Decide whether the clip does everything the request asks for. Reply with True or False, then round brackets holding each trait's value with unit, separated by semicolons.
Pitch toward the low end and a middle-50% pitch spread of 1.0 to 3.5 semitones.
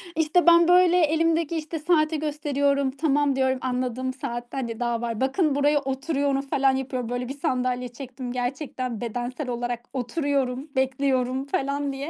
False (270 Hz; 2.8 semitones)